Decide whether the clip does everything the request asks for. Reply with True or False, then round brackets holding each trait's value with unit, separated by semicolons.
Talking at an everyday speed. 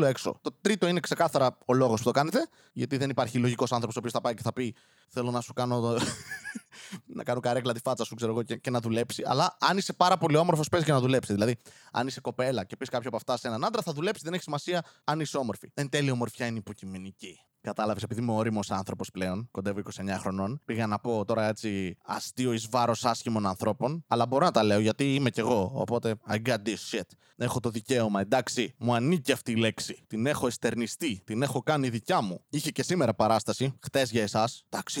False (225 wpm)